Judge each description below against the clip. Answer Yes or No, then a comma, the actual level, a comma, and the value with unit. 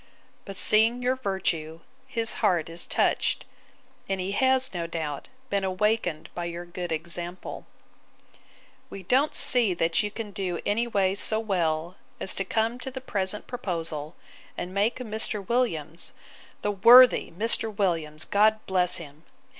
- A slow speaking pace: No, average, 145 wpm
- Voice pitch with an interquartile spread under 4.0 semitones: No, average, 4.6 semitones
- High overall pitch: Yes, high, 195 Hz